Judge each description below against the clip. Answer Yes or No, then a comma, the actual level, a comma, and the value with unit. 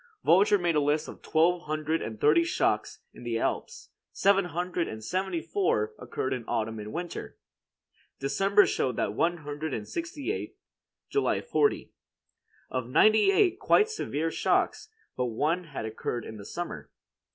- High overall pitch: No, medium, 160 Hz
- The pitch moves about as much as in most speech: No, wide, 7.2 semitones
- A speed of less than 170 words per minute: Yes, average, 155 wpm